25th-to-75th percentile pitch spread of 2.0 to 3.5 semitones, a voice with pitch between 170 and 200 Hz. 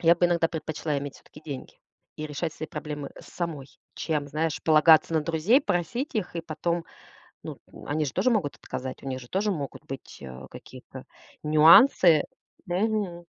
No: average, 2.9 semitones; medium, 160 Hz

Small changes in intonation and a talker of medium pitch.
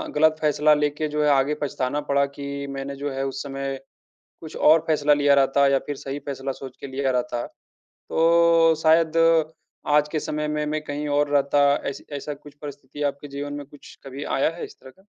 Yes: narrow, 1.5 semitones; medium, 145 Hz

